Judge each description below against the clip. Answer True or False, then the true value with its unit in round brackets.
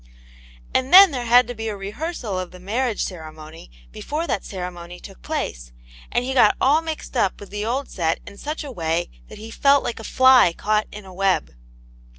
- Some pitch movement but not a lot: False (6.2 semitones)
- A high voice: True (215 Hz)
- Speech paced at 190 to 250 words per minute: True (200 wpm)